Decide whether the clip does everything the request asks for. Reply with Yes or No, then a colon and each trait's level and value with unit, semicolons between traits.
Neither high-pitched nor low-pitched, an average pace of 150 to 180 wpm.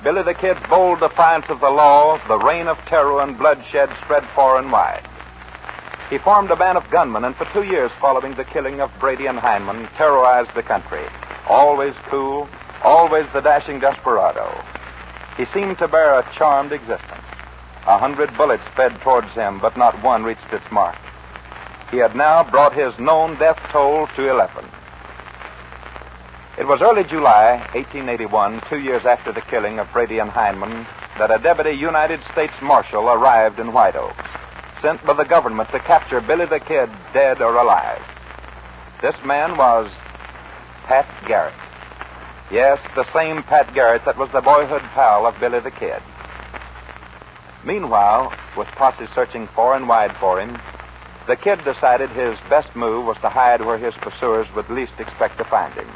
No: low, 125 Hz; average, 165 wpm